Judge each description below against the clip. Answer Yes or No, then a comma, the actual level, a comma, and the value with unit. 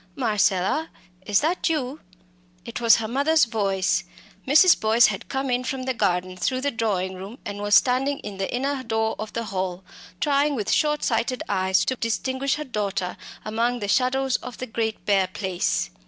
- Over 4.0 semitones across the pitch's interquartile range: Yes, average, 4.8 semitones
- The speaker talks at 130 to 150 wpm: No, average, 175 wpm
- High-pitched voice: Yes, high, 230 Hz